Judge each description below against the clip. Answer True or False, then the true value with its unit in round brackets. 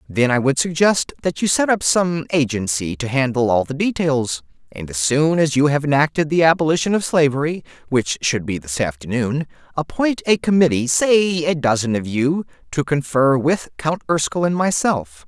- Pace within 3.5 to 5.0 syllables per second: True (4.9 syllables/s)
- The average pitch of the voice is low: False (145 Hz)